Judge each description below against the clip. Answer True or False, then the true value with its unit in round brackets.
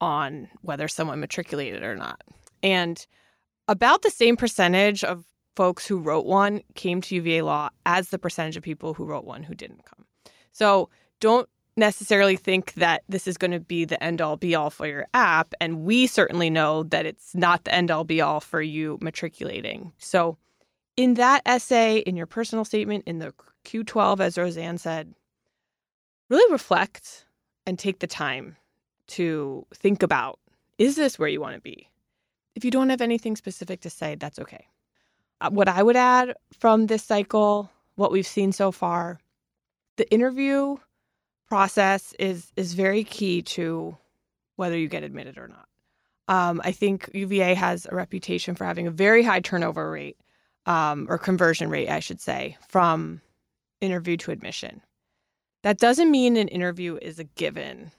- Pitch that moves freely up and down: False (4.1 semitones)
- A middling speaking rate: True (170 wpm)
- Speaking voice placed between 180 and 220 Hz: True (185 Hz)